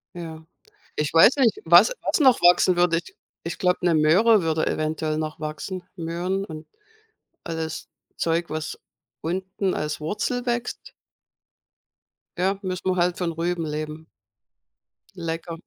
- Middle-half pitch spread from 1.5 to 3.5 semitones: Yes, average, 2.8 semitones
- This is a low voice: No, medium, 170 Hz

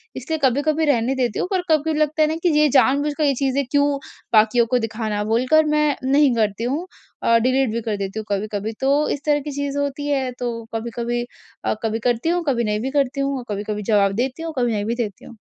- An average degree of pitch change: Yes, average, 4.4 semitones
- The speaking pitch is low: No, very high, 260 Hz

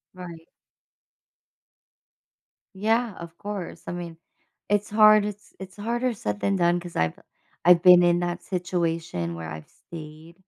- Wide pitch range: No, average, 3.6 semitones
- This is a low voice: No, medium, 175 Hz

